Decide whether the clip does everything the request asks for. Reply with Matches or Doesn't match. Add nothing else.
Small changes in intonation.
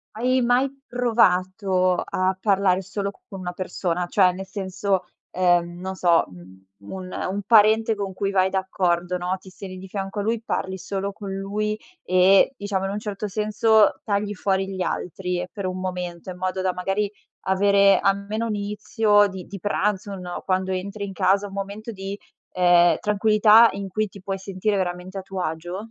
Matches